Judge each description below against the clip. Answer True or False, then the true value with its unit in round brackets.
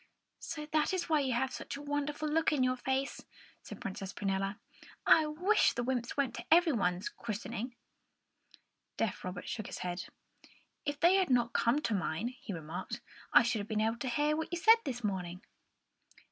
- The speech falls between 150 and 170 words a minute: False (190 wpm)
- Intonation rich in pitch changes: True (6.3 semitones)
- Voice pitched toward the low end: False (250 Hz)